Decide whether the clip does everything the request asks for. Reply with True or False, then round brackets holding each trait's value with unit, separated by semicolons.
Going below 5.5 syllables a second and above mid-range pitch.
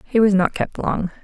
True (4.8 syllables/s; 200 Hz)